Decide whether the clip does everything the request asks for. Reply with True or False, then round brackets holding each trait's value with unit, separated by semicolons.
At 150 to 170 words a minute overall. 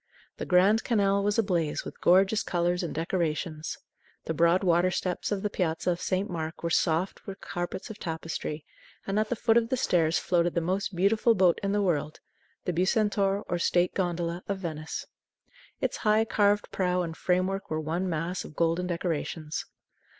False (180 wpm)